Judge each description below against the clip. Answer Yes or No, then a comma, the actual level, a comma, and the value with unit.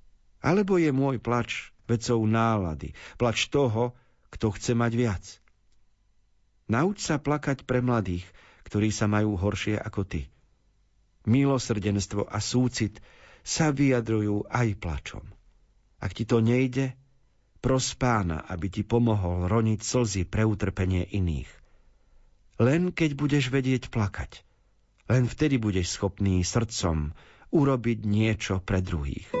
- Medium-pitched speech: No, low, 110 Hz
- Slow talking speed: No, average, 120 wpm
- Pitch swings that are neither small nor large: Yes, average, 4.1 semitones